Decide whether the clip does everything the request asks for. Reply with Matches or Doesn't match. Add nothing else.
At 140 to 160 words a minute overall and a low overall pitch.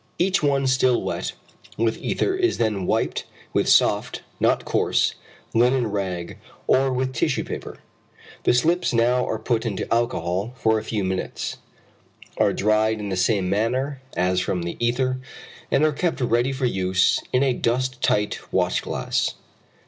Matches